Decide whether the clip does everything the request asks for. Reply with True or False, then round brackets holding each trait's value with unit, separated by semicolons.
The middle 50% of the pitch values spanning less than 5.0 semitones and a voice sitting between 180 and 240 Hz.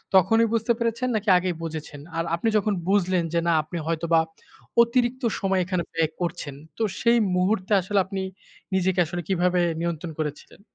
True (4.2 semitones; 185 Hz)